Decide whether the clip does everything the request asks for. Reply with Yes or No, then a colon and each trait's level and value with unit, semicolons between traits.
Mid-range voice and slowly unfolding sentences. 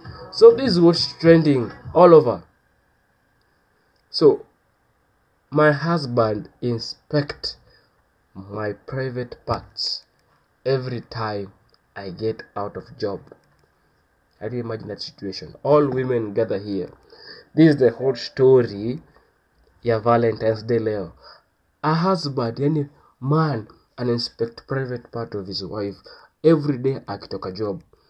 No: low, 120 Hz; slow, 115 wpm